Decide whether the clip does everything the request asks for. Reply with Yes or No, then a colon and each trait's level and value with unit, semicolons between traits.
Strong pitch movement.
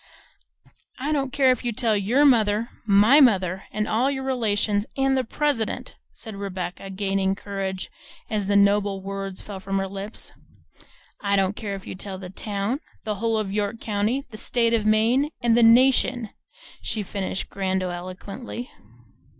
No: average, 3.4 semitones